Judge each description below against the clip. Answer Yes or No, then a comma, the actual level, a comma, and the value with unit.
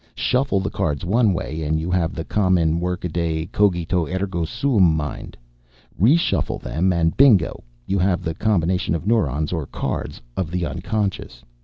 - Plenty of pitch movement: No, average, 3.2 semitones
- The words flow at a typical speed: Yes, average, 155 wpm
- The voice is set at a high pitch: No, very low, 90 Hz